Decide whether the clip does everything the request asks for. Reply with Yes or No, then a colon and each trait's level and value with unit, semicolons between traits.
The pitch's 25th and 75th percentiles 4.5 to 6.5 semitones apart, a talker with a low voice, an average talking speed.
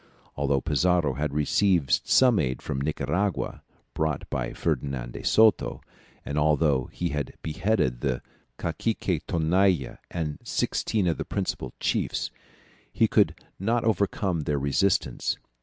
No: wide, 5.6 semitones; very low, 75 Hz; slow, 125 wpm